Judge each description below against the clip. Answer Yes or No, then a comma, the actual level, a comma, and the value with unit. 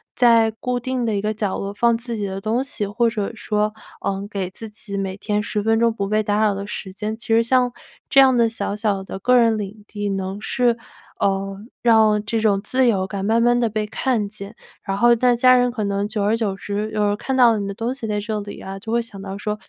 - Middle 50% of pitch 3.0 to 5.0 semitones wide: No, narrow, 2.6 semitones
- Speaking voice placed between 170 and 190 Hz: No, high, 215 Hz